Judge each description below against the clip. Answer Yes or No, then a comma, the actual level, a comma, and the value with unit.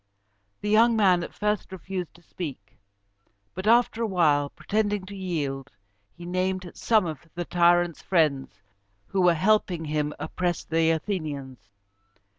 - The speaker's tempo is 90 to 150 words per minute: Yes, average, 140 wpm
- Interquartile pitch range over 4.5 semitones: No, average, 3.8 semitones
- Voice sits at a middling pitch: Yes, medium, 175 Hz